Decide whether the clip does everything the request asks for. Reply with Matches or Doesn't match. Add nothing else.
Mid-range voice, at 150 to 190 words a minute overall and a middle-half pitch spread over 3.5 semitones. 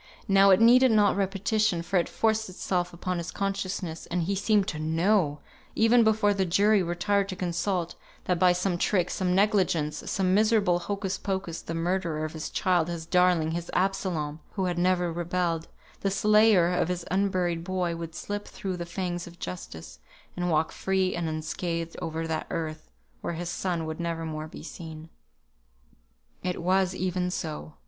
Doesn't match